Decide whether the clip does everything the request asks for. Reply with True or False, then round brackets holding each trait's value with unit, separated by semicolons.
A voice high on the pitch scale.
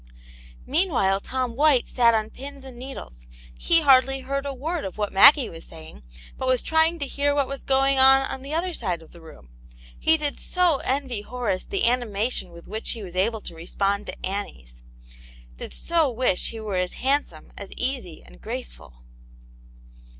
True (250 Hz)